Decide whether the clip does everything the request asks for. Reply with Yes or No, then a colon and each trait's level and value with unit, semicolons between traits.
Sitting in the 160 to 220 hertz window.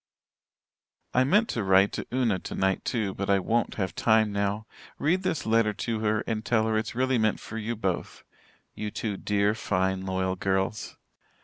No: low, 105 Hz